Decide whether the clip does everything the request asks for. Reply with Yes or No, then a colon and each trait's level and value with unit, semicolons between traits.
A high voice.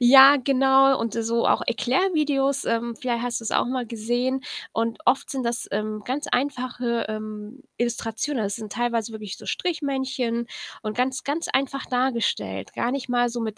Yes: high, 245 Hz